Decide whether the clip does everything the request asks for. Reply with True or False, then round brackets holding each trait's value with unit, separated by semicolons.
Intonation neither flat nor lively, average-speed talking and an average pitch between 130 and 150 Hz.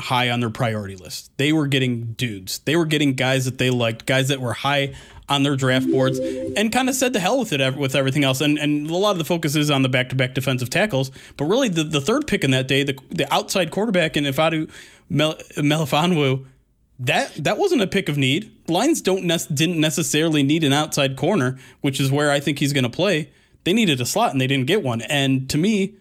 False (3.4 semitones; 235 wpm; 140 Hz)